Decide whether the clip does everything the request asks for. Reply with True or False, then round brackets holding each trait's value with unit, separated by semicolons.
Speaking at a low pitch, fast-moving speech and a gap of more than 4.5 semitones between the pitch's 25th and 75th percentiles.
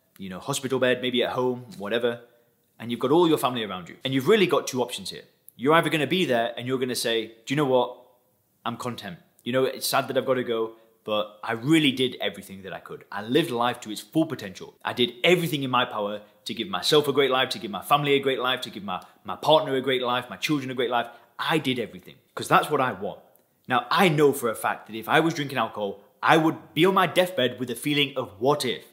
False (125 Hz; 260 wpm; 3.9 semitones)